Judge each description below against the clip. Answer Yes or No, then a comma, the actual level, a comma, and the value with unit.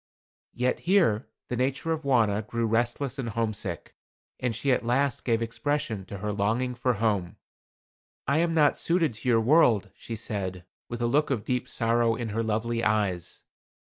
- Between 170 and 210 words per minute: Yes, average, 175 wpm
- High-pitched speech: No, low, 115 Hz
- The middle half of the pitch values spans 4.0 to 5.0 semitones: No, average, 3.2 semitones